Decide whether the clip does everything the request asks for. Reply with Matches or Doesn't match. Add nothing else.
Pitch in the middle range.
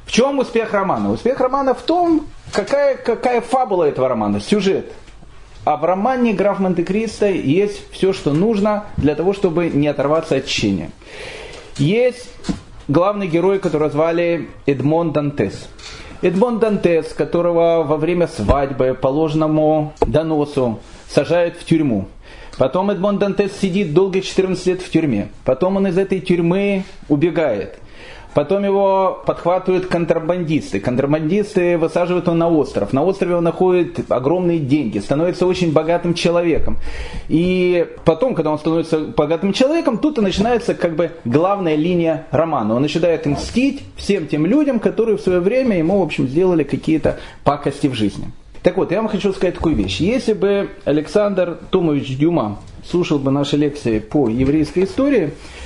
Matches